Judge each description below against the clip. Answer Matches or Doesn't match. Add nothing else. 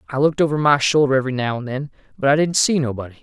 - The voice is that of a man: Matches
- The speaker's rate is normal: Doesn't match